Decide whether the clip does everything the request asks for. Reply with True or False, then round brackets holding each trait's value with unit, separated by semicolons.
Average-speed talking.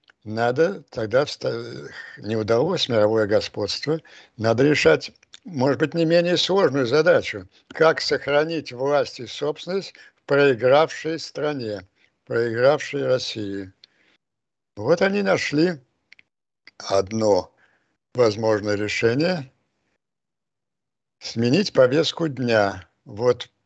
False (85 wpm)